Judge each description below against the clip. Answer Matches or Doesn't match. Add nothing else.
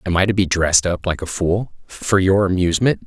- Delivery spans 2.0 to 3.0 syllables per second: Doesn't match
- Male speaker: Matches